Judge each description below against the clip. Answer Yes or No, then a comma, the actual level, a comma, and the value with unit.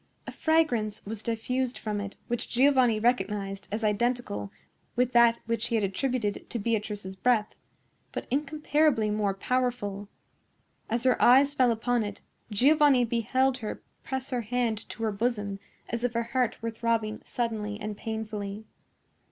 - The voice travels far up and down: No, average, 3.0 semitones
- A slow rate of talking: No, average, 150 wpm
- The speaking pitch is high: Yes, high, 230 Hz